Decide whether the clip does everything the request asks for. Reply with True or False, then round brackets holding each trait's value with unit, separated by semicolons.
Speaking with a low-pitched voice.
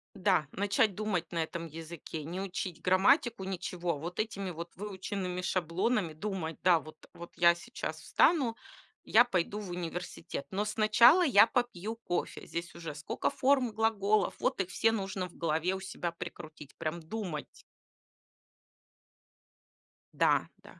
False (185 Hz)